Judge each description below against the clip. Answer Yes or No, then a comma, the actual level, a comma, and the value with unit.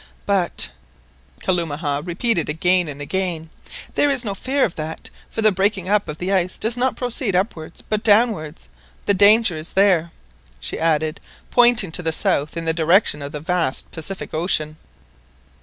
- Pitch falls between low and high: Yes, medium, 180 Hz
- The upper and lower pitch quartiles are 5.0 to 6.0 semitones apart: No, average, 4.5 semitones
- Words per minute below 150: No, average, 160 wpm